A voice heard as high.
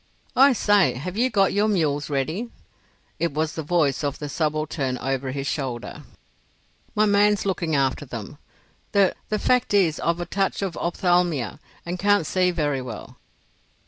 No: medium, 165 Hz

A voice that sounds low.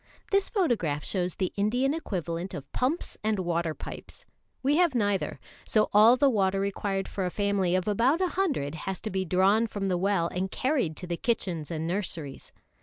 No: high, 195 Hz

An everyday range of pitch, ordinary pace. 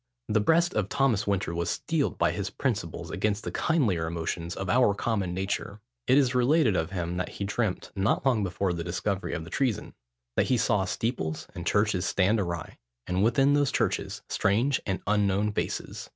Yes: average, 4.6 semitones; average, 185 wpm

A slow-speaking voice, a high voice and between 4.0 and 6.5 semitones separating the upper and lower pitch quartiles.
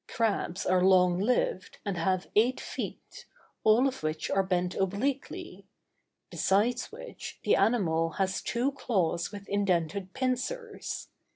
Yes: slow, 125 wpm; high, 200 Hz; average, 5.2 semitones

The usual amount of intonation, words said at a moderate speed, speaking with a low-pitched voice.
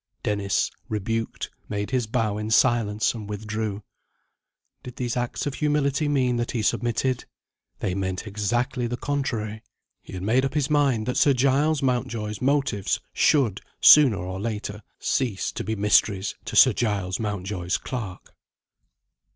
Yes: average, 3.9 semitones; average, 145 wpm; low, 115 Hz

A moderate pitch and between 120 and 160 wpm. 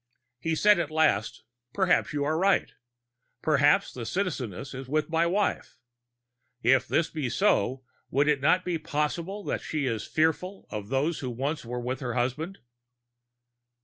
Yes: medium, 150 Hz; average, 155 wpm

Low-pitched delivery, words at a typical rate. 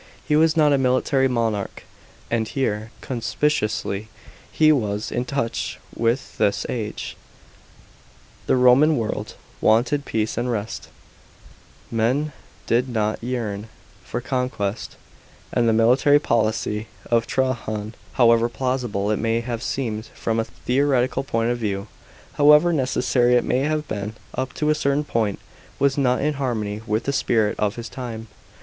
Yes: low, 120 Hz; average, 145 wpm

